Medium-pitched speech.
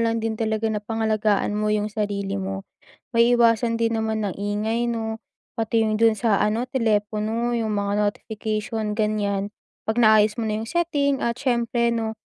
No: high, 220 Hz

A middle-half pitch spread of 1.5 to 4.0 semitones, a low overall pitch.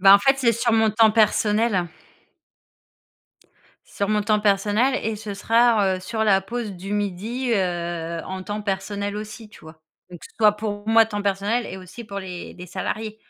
No: narrow, 2.5 semitones; high, 210 Hz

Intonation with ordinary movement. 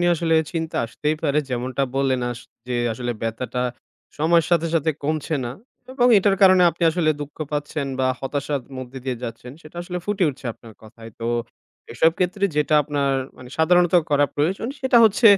Yes: average, 5.0 semitones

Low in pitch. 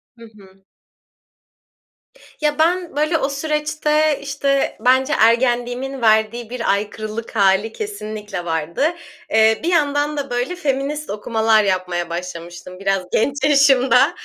No: high, 245 Hz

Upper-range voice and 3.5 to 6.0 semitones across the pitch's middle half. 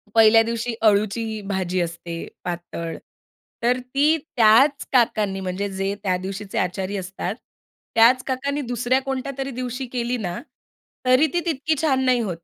Yes: high, 230 Hz; average, 5.0 semitones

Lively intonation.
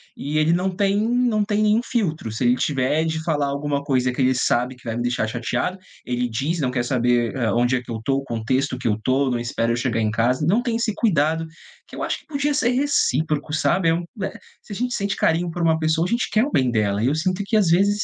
Yes: wide, 7.7 semitones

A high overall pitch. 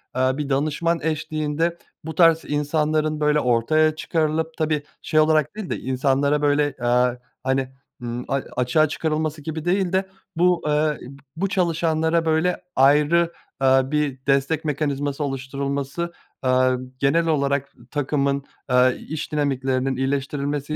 No: medium, 150 Hz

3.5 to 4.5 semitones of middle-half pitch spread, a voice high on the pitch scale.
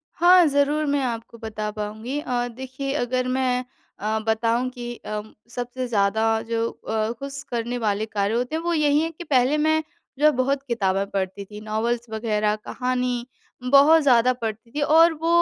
Yes: average, 4.2 semitones; high, 245 Hz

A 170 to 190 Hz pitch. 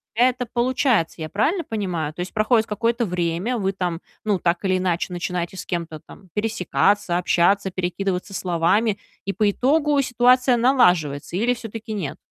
No: high, 200 Hz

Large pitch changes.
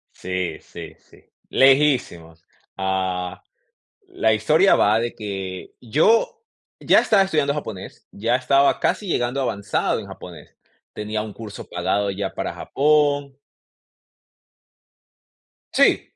Yes: wide, 6.6 semitones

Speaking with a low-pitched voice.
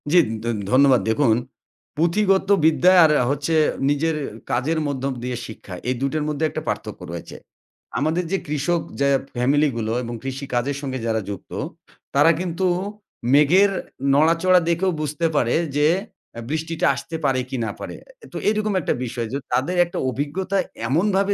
No: medium, 145 Hz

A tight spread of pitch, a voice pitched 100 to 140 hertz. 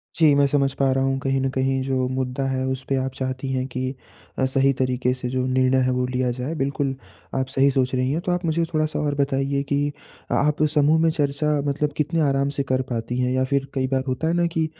Yes: narrow, 1.8 semitones; low, 135 Hz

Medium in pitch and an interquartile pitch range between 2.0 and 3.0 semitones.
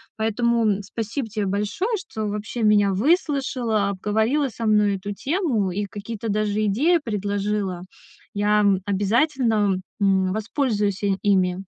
No: high, 210 Hz; narrow, 2.5 semitones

